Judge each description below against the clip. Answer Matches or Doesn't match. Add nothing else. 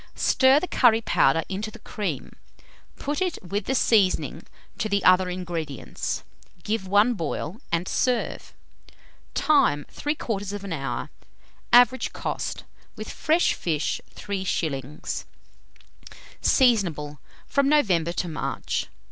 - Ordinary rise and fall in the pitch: Doesn't match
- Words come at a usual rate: Doesn't match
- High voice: Matches